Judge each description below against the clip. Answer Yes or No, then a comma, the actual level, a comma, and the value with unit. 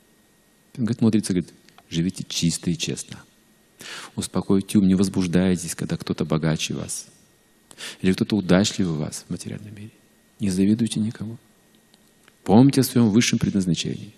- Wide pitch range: No, average, 3.1 semitones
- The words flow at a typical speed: Yes, average, 125 wpm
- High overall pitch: No, low, 100 Hz